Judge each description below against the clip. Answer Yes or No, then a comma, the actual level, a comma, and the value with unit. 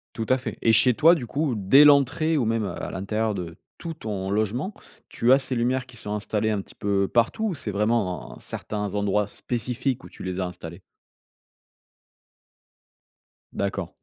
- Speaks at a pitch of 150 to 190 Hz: No, low, 110 Hz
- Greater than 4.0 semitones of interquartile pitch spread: Yes, average, 4.5 semitones